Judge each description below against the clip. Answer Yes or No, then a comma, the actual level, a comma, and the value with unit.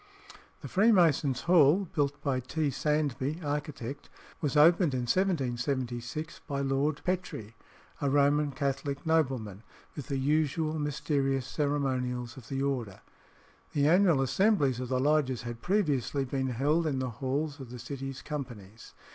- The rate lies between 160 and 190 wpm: No, average, 140 wpm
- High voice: No, medium, 140 Hz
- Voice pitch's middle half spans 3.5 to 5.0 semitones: No, average, 3.0 semitones